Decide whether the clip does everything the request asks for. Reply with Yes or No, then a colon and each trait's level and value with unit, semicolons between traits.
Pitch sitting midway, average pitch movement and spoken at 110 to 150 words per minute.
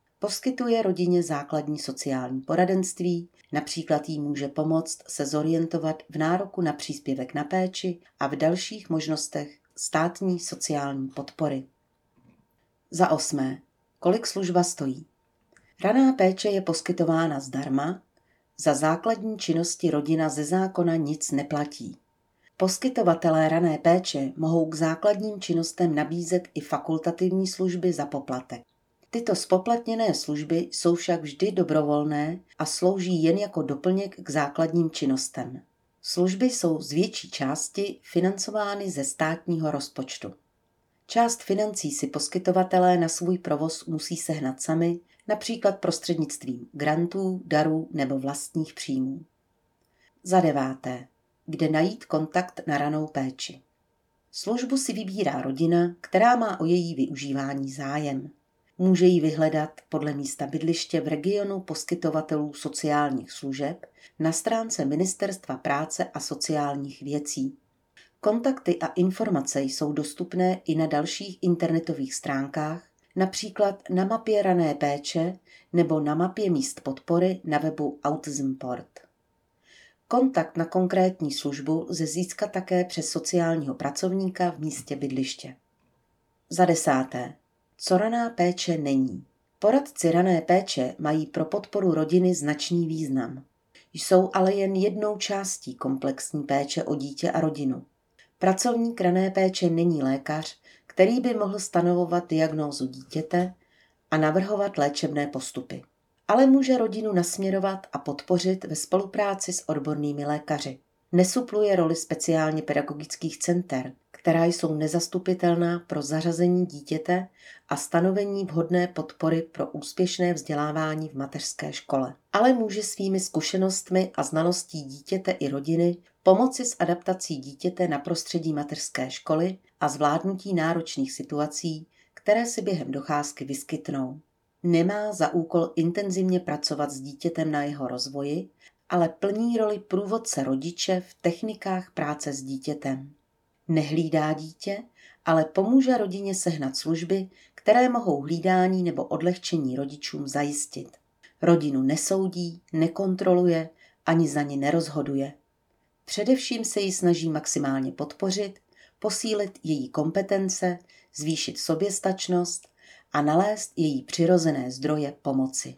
Yes: medium, 165 Hz; average, 4.0 semitones; average, 120 wpm